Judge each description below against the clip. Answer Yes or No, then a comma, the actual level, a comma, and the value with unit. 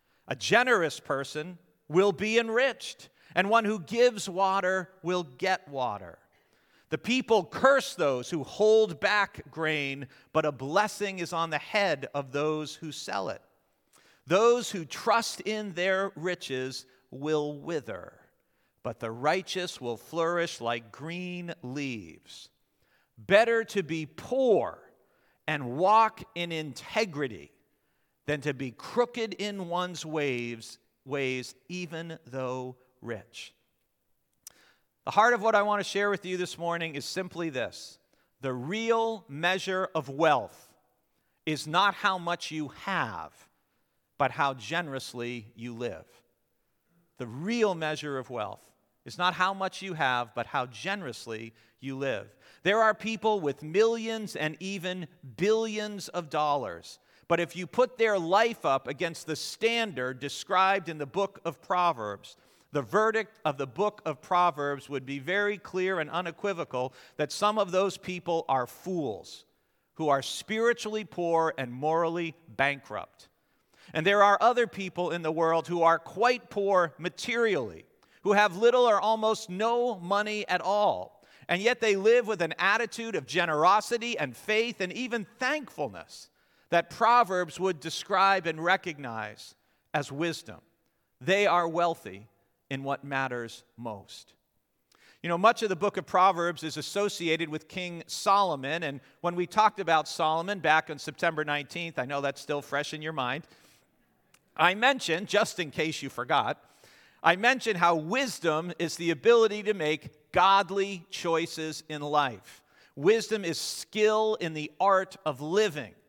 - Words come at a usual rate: Yes, average, 145 wpm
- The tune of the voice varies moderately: No, wide, 5.8 semitones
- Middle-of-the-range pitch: Yes, medium, 170 Hz